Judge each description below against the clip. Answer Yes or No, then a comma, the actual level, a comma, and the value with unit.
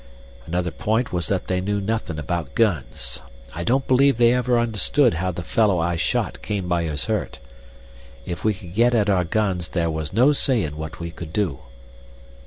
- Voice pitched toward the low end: Yes, very low, 95 Hz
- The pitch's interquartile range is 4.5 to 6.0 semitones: Yes, average, 5.2 semitones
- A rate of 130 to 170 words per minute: No, average, 190 wpm